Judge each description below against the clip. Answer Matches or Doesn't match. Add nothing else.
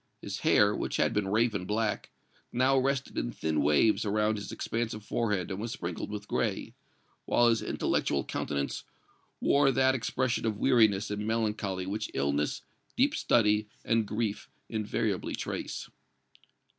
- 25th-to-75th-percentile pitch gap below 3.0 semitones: Matches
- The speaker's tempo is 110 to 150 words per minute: Matches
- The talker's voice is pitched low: Matches